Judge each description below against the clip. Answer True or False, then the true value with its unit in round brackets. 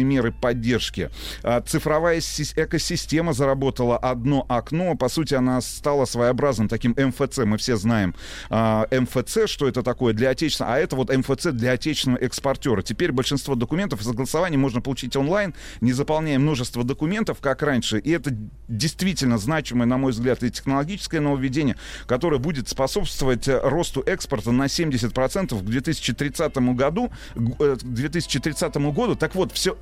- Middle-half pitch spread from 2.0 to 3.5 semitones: False (3.9 semitones)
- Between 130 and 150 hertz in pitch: True (135 Hz)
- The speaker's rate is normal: True (140 wpm)